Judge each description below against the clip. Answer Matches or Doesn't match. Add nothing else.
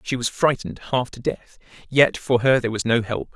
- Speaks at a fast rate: Matches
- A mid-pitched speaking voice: Doesn't match